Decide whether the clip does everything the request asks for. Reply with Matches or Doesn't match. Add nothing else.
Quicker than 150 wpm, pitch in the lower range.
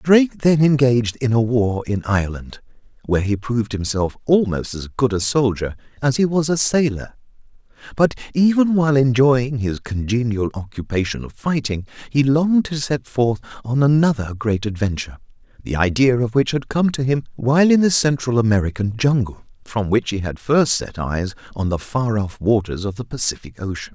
Matches